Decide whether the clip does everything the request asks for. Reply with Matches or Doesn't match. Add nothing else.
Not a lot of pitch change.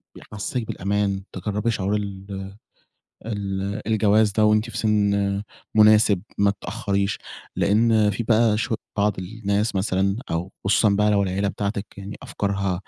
Matches